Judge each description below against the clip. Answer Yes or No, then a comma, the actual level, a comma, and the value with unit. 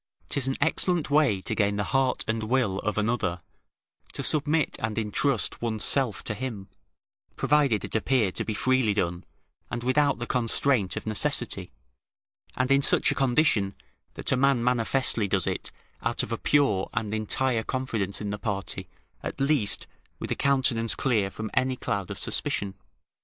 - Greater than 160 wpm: Yes, average, 170 wpm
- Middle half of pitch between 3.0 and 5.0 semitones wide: Yes, average, 4.4 semitones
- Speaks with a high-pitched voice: No, low, 115 Hz